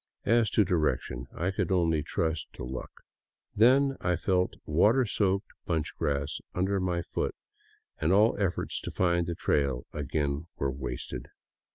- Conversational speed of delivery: Yes, average, 145 wpm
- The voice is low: Yes, very low, 85 Hz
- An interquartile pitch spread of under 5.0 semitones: No, average, 5.3 semitones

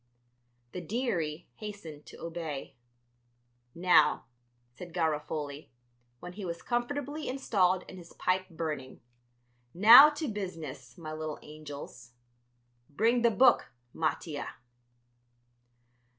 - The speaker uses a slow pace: Yes, slow, 100 wpm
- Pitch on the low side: No, medium, 175 Hz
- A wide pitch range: Yes, wide, 5.7 semitones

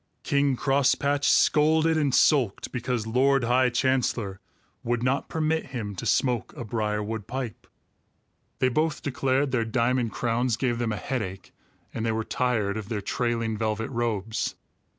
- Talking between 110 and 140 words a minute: No, average, 150 wpm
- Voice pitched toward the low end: Yes, low, 120 Hz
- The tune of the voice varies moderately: Yes, average, 3.3 semitones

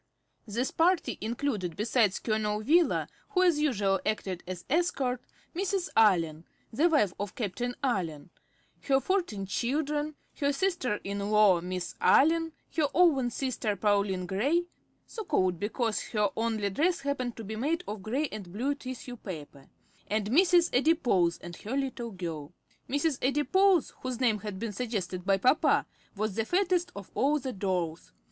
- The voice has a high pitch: Yes, high, 230 Hz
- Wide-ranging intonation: Yes, wide, 6.9 semitones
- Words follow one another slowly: No, average, 155 wpm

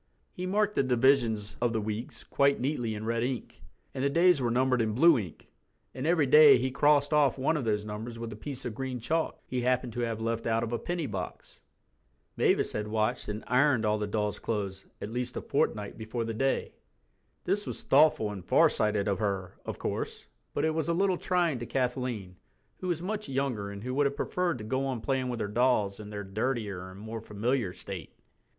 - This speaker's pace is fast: Yes, fast, 215 wpm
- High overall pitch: No, low, 120 Hz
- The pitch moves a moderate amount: Yes, average, 4.5 semitones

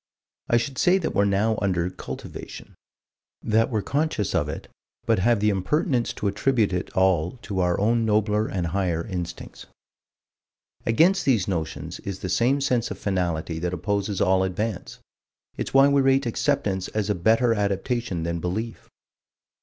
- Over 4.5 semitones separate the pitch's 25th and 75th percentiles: No, average, 4.2 semitones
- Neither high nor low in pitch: No, low, 105 Hz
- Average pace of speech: Yes, average, 160 wpm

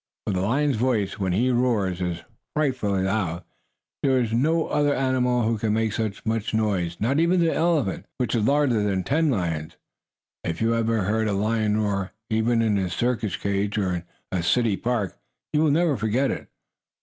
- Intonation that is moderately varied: Yes, average, 4.4 semitones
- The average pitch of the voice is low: Yes, low, 110 Hz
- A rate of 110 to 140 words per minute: No, average, 190 wpm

